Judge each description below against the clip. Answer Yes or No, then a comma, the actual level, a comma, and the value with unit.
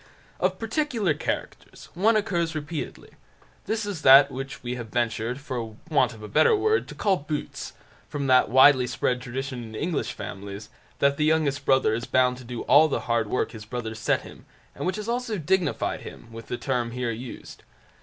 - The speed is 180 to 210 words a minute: Yes, average, 190 wpm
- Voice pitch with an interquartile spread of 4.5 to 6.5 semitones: Yes, average, 5.3 semitones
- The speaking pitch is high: No, low, 135 Hz